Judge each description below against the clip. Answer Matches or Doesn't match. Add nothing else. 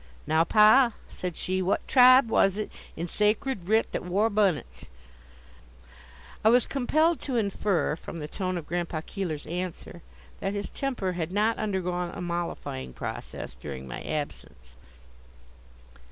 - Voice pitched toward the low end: Doesn't match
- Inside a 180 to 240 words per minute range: Doesn't match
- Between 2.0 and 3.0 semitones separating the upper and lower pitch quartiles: Doesn't match